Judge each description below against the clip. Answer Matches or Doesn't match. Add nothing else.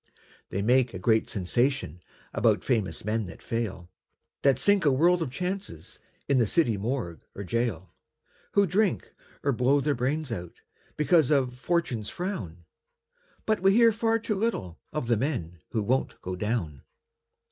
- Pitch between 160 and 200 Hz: Doesn't match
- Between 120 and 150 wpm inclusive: Doesn't match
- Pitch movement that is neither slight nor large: Doesn't match